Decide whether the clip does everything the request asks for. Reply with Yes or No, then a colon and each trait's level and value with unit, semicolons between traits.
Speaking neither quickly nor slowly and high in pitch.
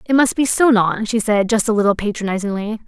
No: fast, 230 wpm; high, 215 Hz